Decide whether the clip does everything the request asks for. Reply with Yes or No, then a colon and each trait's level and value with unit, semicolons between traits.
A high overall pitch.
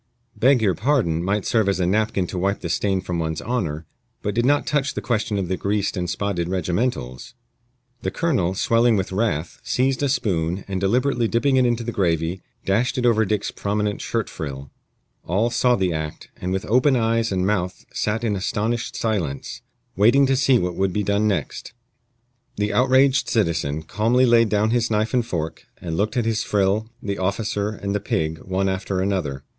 No: low, 105 Hz